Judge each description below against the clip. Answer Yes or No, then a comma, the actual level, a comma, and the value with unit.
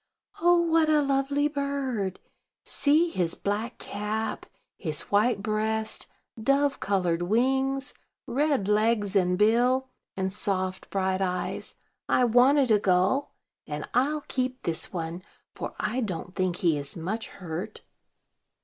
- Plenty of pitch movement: Yes, wide, 6.3 semitones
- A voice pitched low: No, high, 220 Hz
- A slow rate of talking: Yes, slow, 130 wpm